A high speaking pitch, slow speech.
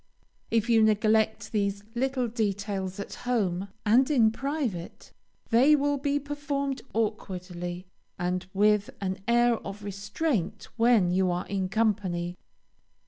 Yes: high, 215 Hz; slow, 125 wpm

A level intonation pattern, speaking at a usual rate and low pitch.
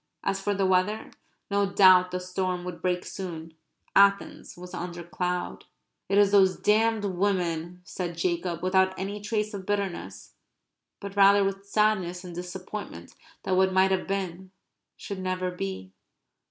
No: narrow, 1.8 semitones; average, 150 wpm; medium, 185 Hz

